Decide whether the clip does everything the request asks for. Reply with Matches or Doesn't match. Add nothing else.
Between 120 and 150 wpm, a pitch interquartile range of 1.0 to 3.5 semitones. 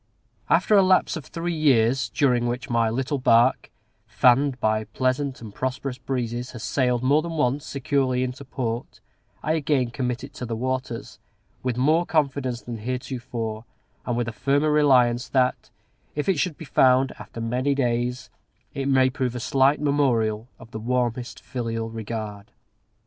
Doesn't match